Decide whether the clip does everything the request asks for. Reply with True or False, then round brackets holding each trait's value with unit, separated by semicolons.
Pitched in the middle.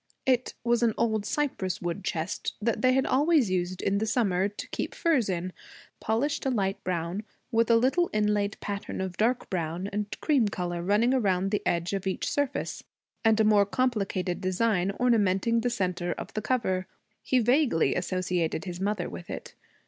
False (205 Hz)